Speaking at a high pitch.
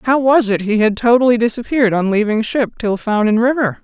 Yes: high, 230 Hz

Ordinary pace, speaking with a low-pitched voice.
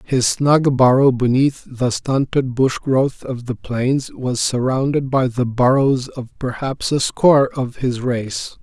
Yes: average, 160 wpm; low, 130 Hz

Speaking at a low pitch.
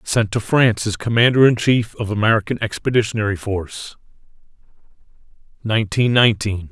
Yes: low, 110 Hz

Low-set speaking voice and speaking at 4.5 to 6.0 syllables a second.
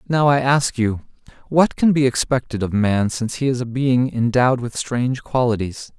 Yes: low, 125 Hz; 5.1 syllables/s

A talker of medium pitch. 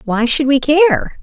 No: very high, 290 Hz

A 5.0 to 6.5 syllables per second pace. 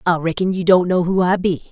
Yes: 5.9 syllables/s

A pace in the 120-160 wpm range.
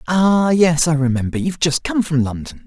No: average, 200 wpm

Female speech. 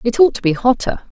Yes: female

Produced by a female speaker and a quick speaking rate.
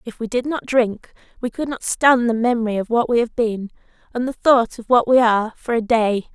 Yes: female; fast, 245 wpm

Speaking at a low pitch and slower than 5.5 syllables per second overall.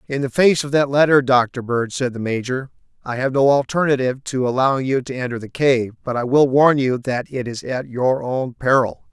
Yes: low, 130 Hz; 5.2 syllables/s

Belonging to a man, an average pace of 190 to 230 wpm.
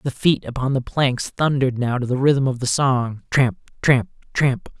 Yes: male; average, 200 wpm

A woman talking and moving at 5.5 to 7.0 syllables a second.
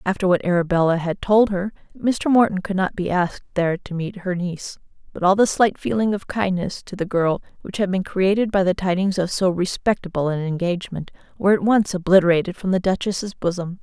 Yes: female; 5.7 syllables/s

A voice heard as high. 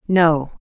No: medium, 165 Hz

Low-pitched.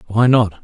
Yes: low, 110 Hz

